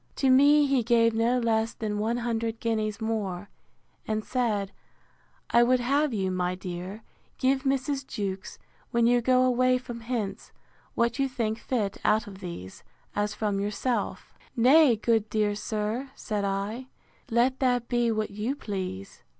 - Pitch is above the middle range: Yes, high, 230 Hz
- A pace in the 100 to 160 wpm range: Yes, average, 150 wpm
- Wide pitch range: No, average, 3.3 semitones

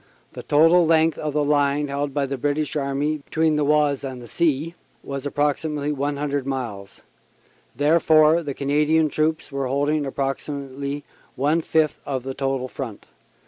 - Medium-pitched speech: Yes, medium, 145 Hz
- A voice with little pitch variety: Yes, narrow, 1.9 semitones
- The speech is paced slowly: No, average, 150 wpm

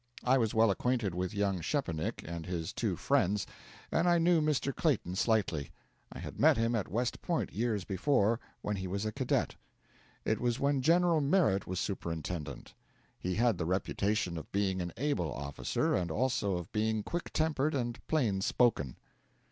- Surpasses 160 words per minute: Yes, average, 170 wpm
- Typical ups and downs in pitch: No, wide, 6.3 semitones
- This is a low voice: Yes, low, 105 Hz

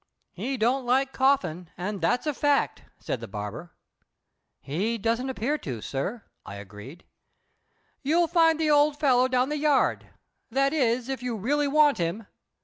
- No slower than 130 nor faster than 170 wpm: Yes, average, 155 wpm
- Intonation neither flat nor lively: No, wide, 7.2 semitones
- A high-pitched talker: Yes, very high, 250 Hz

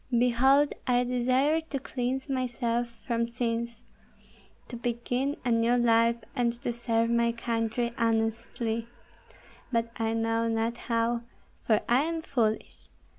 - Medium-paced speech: No, slow, 125 wpm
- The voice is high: Yes, high, 235 Hz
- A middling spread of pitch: No, narrow, 1.4 semitones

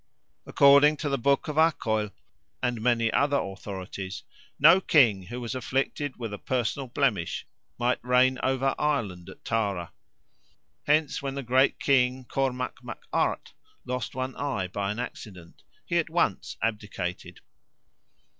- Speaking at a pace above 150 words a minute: No, average, 140 wpm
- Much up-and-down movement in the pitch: No, average, 4.6 semitones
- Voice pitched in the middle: No, low, 125 Hz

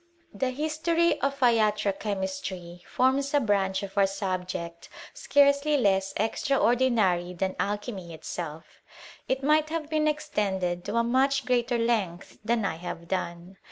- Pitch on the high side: Yes, high, 210 Hz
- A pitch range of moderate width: No, wide, 6.4 semitones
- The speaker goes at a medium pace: No, slow, 130 wpm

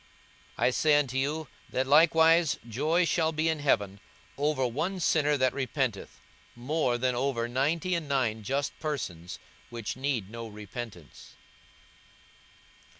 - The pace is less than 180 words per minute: Yes, slow, 135 wpm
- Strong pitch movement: No, average, 4.5 semitones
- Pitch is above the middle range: No, low, 135 Hz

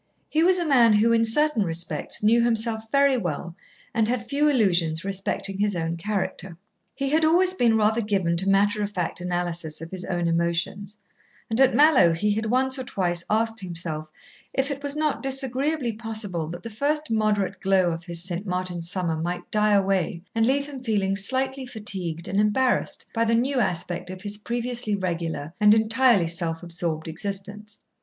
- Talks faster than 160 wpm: Yes, average, 180 wpm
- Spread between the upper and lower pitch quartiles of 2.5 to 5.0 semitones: No, wide, 5.4 semitones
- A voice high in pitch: Yes, high, 205 Hz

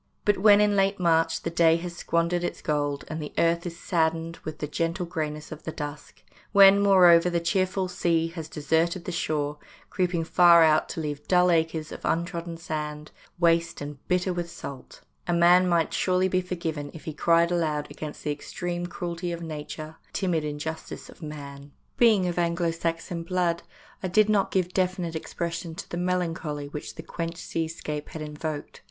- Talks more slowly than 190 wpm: No, average, 195 wpm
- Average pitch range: No, narrow, 2.2 semitones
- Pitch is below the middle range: No, medium, 170 Hz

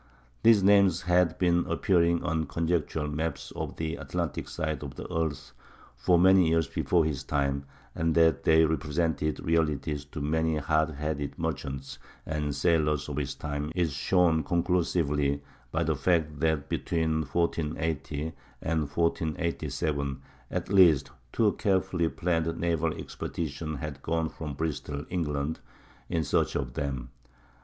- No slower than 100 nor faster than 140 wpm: Yes, slow, 135 wpm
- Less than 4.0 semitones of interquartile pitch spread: Yes, narrow, 2.4 semitones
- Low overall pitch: Yes, very low, 80 Hz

